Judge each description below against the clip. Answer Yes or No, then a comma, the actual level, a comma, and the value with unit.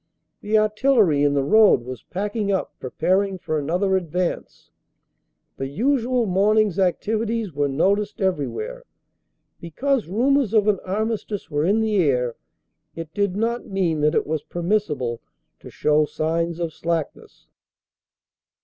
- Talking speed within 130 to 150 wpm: Yes, average, 140 wpm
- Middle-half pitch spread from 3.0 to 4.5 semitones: No, wide, 5.4 semitones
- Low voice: No, high, 190 Hz